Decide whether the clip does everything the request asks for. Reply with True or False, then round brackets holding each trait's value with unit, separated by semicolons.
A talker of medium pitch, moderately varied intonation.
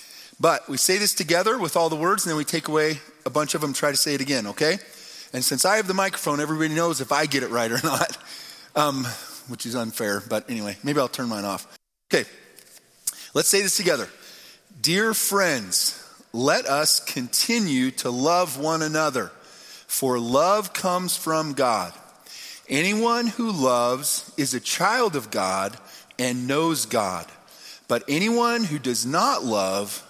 False (155 Hz; 6.4 semitones)